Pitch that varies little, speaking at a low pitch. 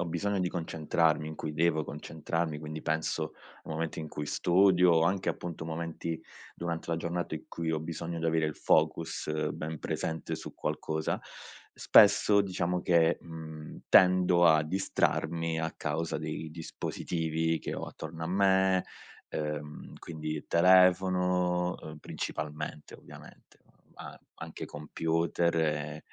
Yes: narrow, 2.0 semitones; very low, 80 Hz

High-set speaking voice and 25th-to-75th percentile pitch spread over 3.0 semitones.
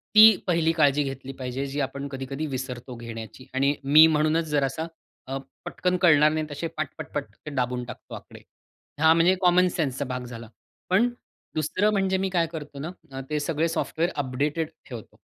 No: medium, 150 Hz; average, 3.8 semitones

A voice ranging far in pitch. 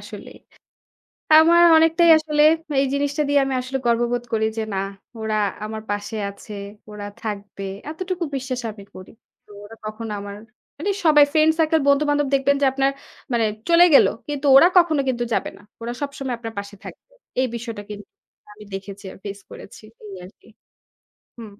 Yes: wide, 5.7 semitones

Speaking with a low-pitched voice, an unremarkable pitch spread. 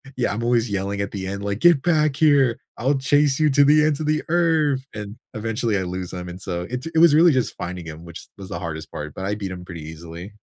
No: low, 110 Hz; wide, 7.9 semitones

